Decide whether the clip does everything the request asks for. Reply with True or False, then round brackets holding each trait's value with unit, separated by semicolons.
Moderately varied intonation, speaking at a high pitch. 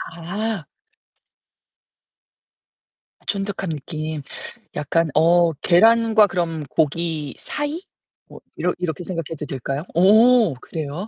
False (4.6 semitones; 170 Hz)